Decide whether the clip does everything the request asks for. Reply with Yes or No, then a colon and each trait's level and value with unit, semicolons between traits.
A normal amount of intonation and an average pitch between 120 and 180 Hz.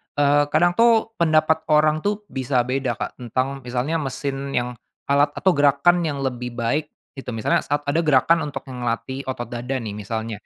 Yes: average, 3.8 semitones; medium, 140 Hz